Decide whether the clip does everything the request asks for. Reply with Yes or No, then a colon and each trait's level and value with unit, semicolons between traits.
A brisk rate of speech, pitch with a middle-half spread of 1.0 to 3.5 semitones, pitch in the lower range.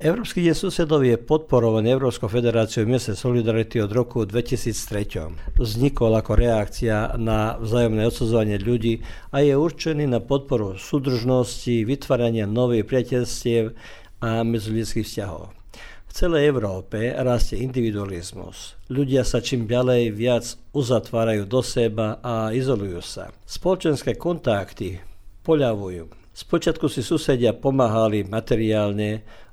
No: slow, 110 wpm; average, 2.9 semitones; low, 115 Hz